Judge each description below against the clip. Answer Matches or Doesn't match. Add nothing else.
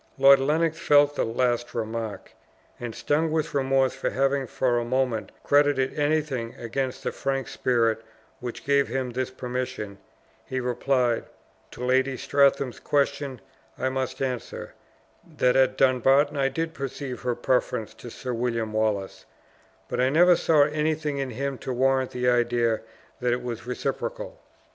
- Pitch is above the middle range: Doesn't match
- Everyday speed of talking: Matches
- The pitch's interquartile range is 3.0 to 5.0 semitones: Doesn't match